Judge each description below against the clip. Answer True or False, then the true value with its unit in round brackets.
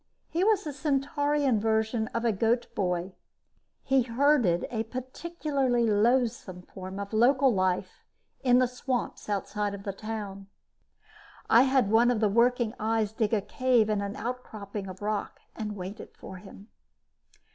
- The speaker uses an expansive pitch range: False (3.9 semitones)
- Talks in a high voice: True (225 Hz)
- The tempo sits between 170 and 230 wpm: False (145 wpm)